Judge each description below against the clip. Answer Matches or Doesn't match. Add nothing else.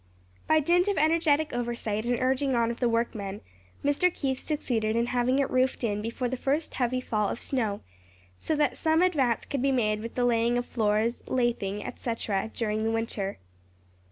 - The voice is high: Matches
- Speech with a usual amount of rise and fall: Matches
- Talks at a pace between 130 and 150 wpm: Doesn't match